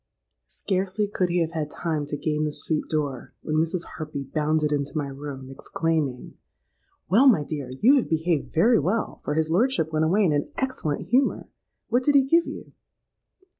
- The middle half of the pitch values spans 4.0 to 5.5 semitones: Yes, average, 5.0 semitones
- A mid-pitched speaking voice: Yes, medium, 160 Hz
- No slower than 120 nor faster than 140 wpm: No, average, 180 wpm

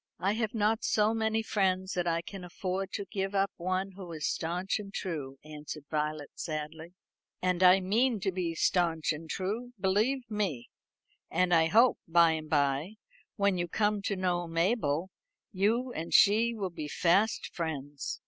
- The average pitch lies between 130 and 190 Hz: Yes, medium, 185 Hz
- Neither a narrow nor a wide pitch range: Yes, average, 4.0 semitones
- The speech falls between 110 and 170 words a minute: Yes, average, 165 wpm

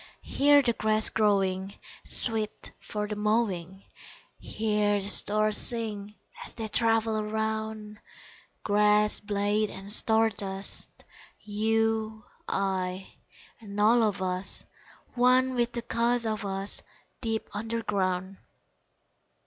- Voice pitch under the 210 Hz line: No, high, 215 Hz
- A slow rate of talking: Yes, slow, 110 wpm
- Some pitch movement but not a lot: No, narrow, 1.8 semitones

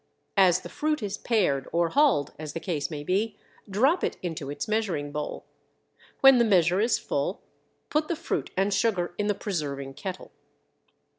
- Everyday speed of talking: Yes, average, 170 wpm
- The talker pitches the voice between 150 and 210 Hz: Yes, high, 190 Hz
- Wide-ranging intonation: Yes, wide, 6.5 semitones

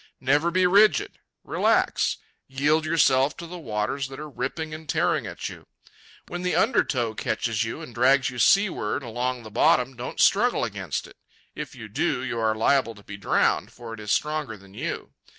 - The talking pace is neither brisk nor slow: Yes, average, 185 wpm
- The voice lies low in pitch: Yes, low, 130 Hz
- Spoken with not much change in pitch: No, wide, 5.5 semitones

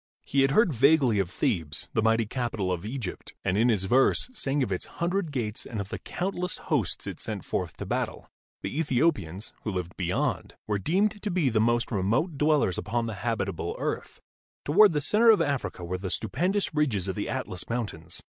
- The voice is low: Yes, low, 120 Hz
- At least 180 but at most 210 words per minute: Yes, average, 195 wpm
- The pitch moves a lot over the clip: Yes, wide, 7.5 semitones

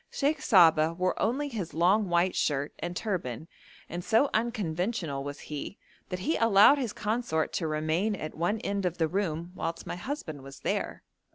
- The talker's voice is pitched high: No, medium, 180 Hz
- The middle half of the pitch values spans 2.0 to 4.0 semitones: No, average, 5.3 semitones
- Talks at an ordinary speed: Yes, average, 175 wpm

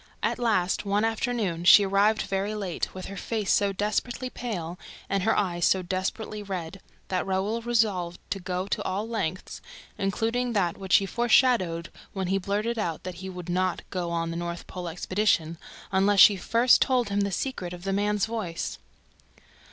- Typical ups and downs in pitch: Yes, average, 3.1 semitones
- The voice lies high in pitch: Yes, high, 195 Hz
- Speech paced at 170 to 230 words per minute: Yes, average, 175 wpm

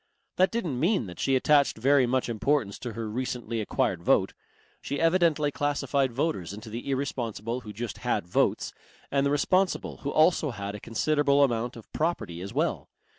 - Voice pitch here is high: No, low, 130 Hz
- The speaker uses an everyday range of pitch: Yes, average, 4.5 semitones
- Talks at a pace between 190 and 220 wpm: No, average, 175 wpm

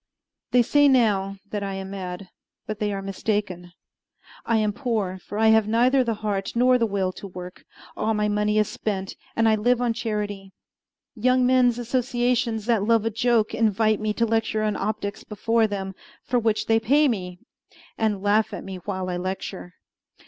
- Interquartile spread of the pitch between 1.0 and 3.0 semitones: Yes, average, 2.7 semitones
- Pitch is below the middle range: No, high, 215 Hz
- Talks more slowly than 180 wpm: No, average, 185 wpm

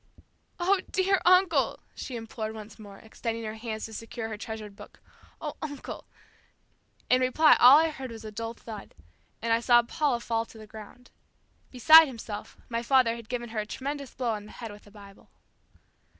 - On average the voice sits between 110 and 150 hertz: No, high, 230 Hz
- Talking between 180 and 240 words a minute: Yes, average, 185 wpm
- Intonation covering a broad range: No, average, 3.1 semitones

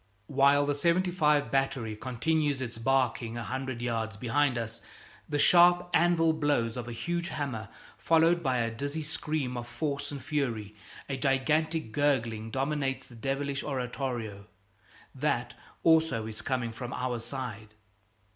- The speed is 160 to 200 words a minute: No, average, 140 wpm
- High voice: No, low, 135 Hz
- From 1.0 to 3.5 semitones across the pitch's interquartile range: No, average, 4.1 semitones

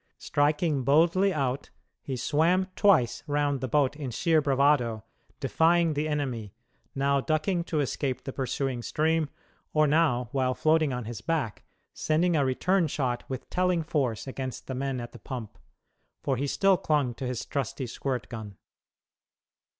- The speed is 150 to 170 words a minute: Yes, average, 155 wpm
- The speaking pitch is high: No, medium, 140 Hz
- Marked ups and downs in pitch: No, average, 3.6 semitones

